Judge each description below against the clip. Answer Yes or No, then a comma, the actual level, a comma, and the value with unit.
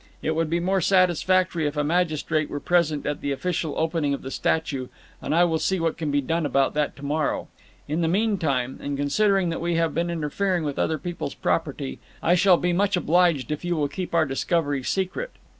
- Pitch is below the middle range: No, medium, 165 Hz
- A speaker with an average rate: No, fast, 210 wpm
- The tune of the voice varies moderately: Yes, average, 3.3 semitones